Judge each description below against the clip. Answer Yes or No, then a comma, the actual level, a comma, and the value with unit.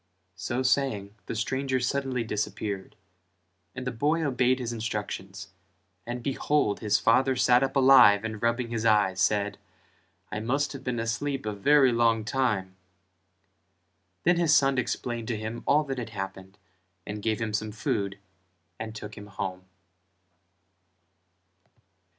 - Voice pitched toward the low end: Yes, low, 115 Hz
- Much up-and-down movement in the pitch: No, average, 3.9 semitones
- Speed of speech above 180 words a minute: No, average, 140 wpm